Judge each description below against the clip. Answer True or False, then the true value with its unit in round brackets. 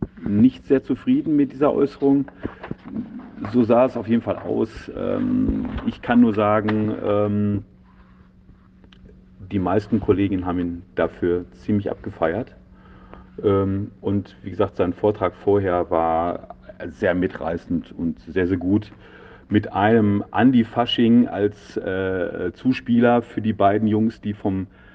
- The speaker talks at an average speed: False (120 wpm)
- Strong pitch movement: False (3.8 semitones)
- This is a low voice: True (105 Hz)